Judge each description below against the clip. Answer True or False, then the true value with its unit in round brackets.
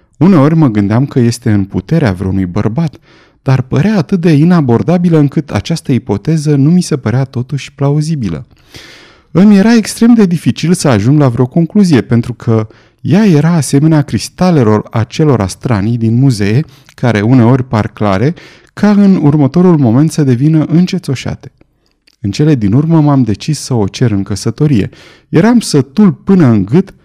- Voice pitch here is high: False (140 Hz)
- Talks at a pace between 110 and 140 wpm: False (155 wpm)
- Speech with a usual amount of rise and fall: False (5.9 semitones)